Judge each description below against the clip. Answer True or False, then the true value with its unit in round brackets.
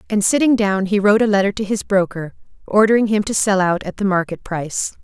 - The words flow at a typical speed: False (225 wpm)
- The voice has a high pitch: True (200 Hz)